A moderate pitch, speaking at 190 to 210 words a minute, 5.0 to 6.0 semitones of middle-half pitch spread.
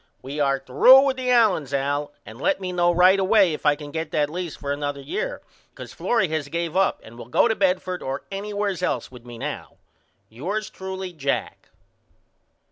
Yes: medium, 170 Hz; average, 195 wpm; wide, 5.4 semitones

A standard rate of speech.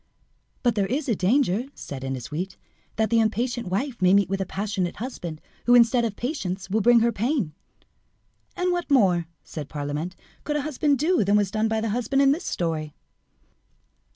Yes: average, 180 wpm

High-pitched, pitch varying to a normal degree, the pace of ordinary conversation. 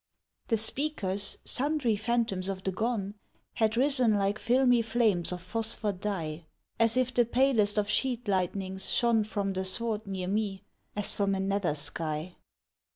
Yes: high, 210 Hz; average, 3.6 semitones; average, 155 wpm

